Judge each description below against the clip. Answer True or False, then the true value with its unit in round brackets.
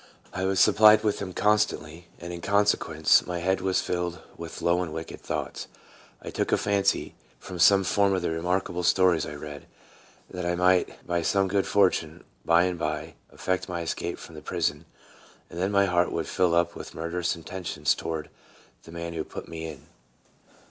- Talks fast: False (185 wpm)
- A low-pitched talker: True (90 Hz)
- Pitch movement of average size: False (2.3 semitones)